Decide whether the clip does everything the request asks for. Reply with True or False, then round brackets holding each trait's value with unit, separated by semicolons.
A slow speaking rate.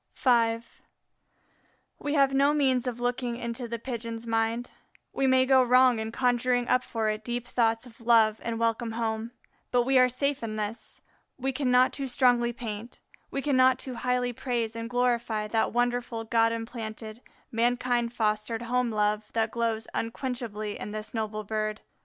False (165 wpm)